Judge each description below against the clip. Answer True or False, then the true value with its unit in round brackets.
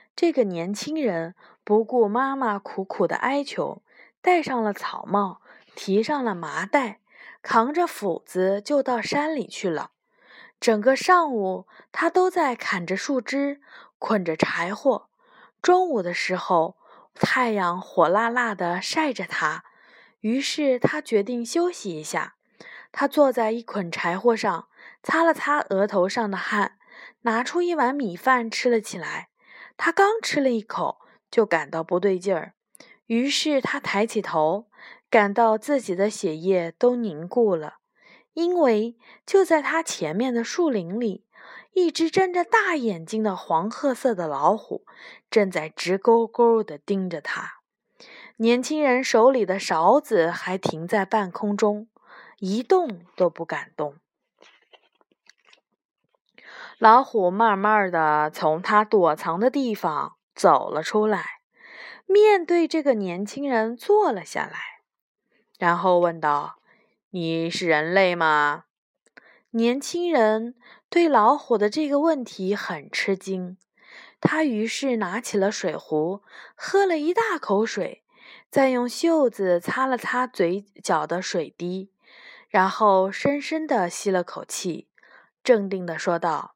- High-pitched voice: True (225 Hz)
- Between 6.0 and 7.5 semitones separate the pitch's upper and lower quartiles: True (6.9 semitones)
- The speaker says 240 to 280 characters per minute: False (190 characters per minute)